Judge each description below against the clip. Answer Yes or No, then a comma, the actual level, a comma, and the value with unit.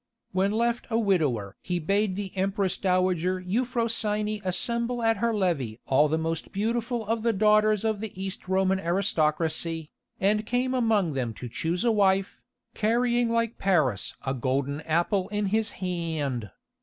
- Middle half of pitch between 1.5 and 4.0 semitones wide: No, average, 5.2 semitones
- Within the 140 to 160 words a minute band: Yes, average, 155 wpm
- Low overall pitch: No, high, 195 Hz